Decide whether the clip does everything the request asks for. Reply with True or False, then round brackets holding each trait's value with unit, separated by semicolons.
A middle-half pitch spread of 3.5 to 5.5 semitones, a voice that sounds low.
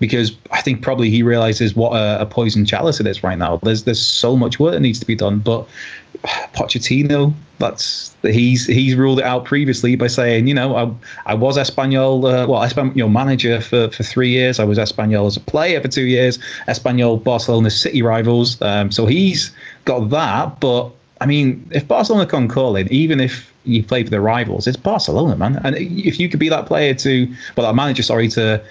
False (2.8 semitones; 125 Hz)